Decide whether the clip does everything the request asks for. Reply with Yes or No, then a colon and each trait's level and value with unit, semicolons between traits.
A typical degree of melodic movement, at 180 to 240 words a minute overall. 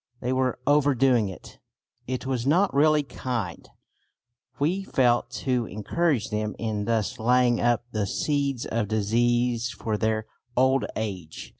No: average, 3.5 semitones; slow, 135 wpm